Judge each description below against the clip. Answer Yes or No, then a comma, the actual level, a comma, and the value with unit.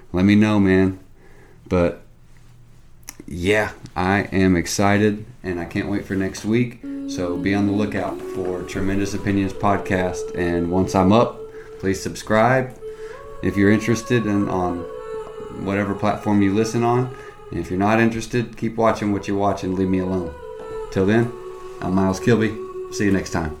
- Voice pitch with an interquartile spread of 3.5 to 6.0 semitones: Yes, average, 4.2 semitones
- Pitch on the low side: Yes, low, 100 Hz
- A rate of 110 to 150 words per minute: No, average, 160 wpm